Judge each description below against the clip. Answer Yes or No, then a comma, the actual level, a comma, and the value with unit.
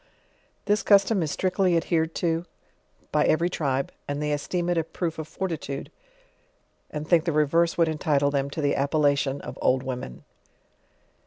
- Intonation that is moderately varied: Yes, average, 3.1 semitones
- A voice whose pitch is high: No, medium, 155 Hz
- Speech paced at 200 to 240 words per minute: No, average, 160 wpm